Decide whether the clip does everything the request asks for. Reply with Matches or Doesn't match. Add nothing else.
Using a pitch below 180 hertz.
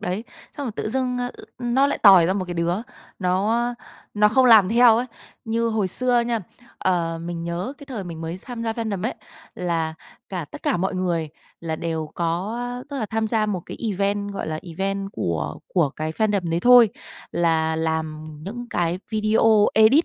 Doesn't match